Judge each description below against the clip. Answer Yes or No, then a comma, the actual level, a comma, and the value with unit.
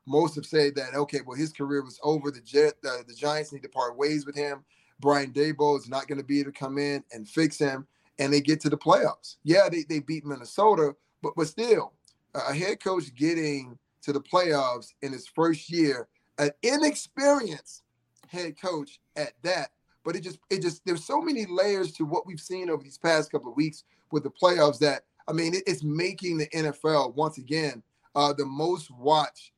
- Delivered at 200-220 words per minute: Yes, fast, 205 wpm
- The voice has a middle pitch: Yes, medium, 150 Hz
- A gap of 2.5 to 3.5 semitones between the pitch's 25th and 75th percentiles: Yes, average, 2.9 semitones